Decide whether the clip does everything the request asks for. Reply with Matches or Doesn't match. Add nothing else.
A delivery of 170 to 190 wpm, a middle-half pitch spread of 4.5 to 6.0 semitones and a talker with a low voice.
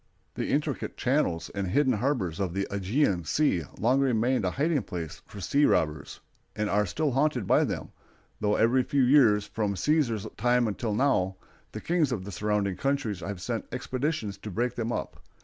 Matches